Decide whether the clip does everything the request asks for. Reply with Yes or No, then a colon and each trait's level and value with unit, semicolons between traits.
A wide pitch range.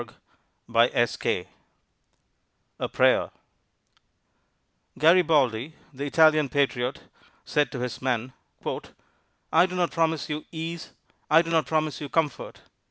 No: average, 3.9 semitones